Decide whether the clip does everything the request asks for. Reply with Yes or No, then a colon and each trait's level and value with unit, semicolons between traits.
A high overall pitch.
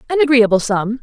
Yes: high, 240 Hz